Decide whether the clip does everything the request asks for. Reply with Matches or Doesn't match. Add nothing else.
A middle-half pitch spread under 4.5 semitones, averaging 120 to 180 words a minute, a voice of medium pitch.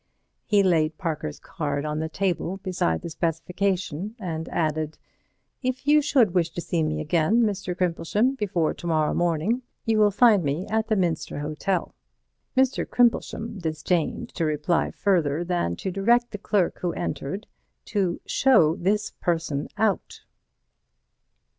Doesn't match